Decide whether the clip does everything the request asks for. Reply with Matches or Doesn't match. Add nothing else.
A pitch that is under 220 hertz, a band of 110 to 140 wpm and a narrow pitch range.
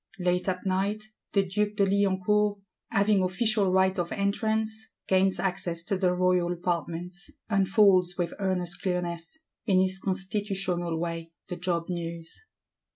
Matches